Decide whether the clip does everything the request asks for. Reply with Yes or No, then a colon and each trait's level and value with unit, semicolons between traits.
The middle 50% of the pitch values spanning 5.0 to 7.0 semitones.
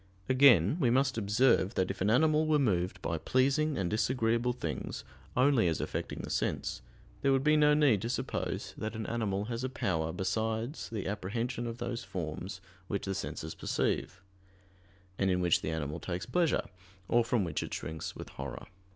Yes: wide, 5.4 semitones